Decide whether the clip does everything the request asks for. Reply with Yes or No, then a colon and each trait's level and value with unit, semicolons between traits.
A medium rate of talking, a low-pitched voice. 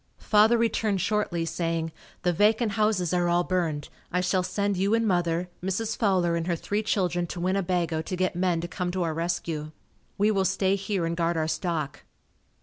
No: average, 190 wpm; medium, 180 Hz